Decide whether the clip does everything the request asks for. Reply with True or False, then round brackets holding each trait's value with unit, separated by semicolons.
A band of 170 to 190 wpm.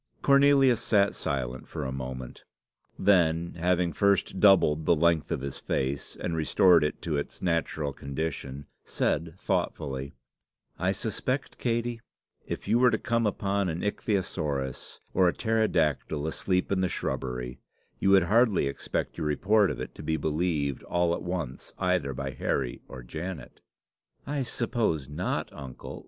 False (150 wpm)